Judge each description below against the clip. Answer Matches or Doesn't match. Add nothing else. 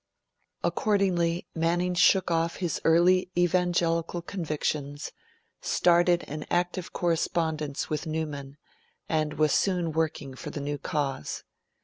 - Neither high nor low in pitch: Matches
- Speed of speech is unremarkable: Doesn't match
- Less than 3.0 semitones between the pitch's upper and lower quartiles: Matches